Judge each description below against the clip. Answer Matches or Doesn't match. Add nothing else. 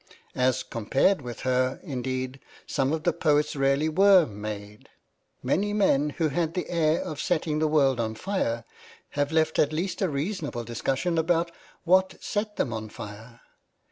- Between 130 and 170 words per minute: Matches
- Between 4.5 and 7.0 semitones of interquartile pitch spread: Matches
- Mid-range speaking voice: Matches